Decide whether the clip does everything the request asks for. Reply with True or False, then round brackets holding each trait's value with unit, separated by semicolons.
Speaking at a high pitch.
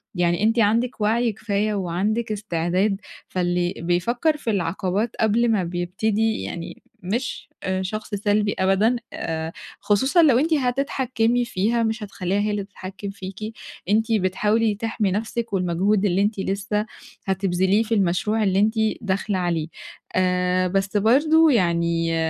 True (205 Hz)